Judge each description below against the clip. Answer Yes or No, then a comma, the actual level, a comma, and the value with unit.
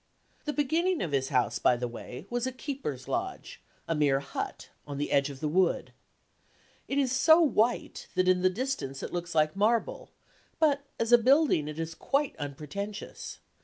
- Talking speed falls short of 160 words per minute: No, average, 180 wpm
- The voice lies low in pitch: No, medium, 185 Hz